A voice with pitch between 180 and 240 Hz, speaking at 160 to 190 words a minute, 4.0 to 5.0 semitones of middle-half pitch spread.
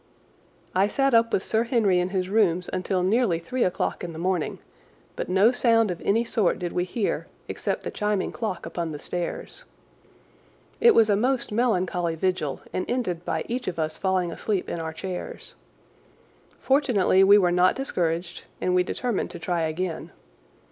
Yes: medium, 185 Hz; average, 175 wpm; average, 4.4 semitones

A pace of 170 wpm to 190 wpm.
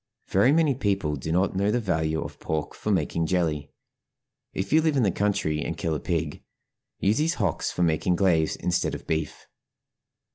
Yes: average, 185 wpm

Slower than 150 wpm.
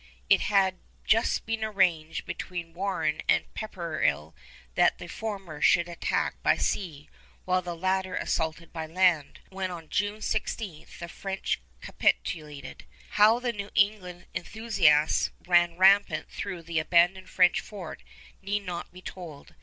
Yes: average, 140 wpm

